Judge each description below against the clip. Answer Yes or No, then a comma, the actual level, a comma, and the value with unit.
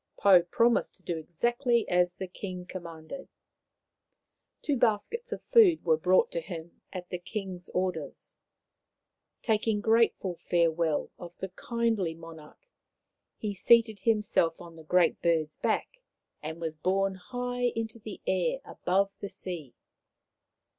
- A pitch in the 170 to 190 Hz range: Yes, medium, 185 Hz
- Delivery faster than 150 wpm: No, average, 140 wpm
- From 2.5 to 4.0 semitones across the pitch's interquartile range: No, average, 4.8 semitones